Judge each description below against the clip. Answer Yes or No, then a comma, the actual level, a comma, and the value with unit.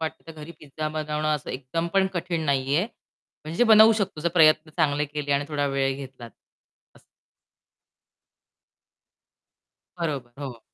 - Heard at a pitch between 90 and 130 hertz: No, medium, 155 Hz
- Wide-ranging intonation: No, average, 2.8 semitones